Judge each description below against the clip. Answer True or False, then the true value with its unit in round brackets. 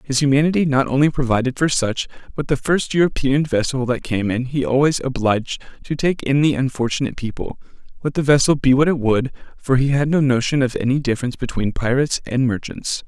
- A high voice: False (135 Hz)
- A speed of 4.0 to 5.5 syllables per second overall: False (6.0 syllables/s)